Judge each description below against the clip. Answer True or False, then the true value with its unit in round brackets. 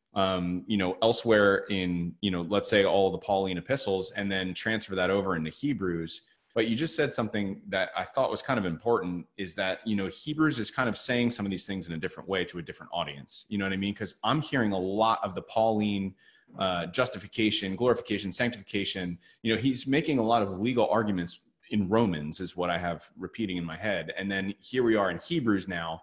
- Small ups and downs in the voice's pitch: False (3.4 semitones)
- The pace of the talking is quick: True (225 wpm)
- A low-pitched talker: True (100 Hz)